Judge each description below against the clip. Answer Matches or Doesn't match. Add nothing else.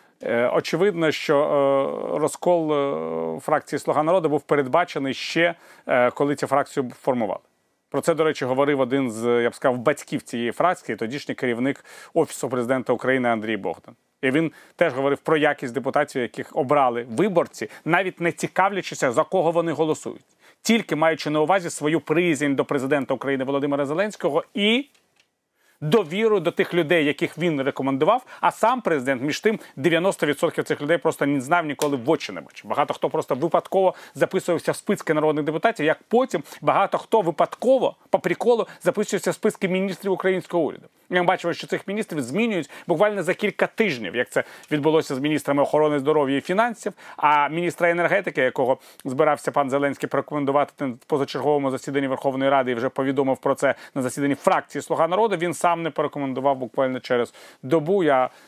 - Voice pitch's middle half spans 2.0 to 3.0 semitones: Doesn't match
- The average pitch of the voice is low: Doesn't match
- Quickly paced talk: Matches